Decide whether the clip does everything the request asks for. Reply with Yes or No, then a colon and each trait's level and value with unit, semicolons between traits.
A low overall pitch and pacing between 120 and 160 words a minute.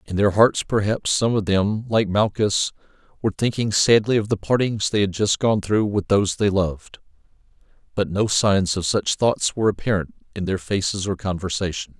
No: low, 100 Hz; average, 185 wpm